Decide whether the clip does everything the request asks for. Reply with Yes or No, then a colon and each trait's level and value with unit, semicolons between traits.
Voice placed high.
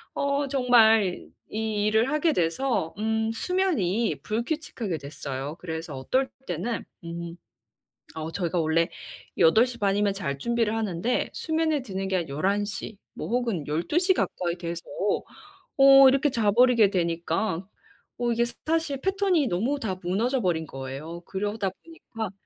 Yes: high, 215 Hz